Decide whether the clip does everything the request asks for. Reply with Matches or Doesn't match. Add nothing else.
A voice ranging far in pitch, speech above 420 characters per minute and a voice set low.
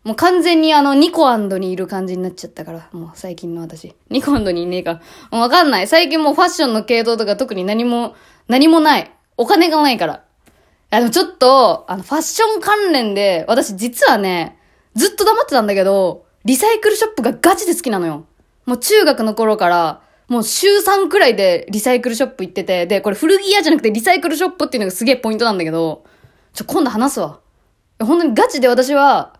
Doesn't match